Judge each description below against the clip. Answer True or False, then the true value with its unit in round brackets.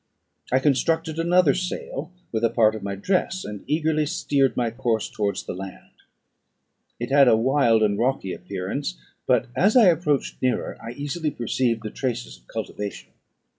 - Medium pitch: False (125 Hz)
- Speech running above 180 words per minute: False (165 wpm)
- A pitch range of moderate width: False (5.8 semitones)